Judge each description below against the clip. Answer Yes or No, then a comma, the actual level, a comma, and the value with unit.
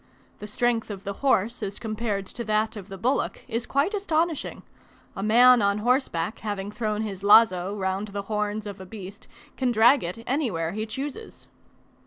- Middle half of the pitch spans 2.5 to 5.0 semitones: Yes, average, 3.4 semitones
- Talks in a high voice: Yes, high, 215 Hz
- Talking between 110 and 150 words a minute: No, average, 175 wpm